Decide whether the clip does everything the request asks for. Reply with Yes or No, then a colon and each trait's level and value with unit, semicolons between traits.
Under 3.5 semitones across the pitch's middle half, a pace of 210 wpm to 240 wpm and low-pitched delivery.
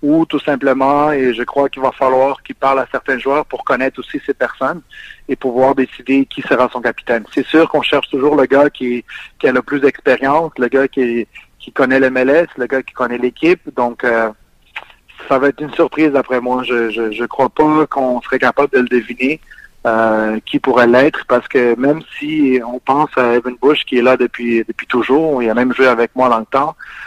Yes: narrow, 2.5 semitones; average, 215 wpm; low, 130 Hz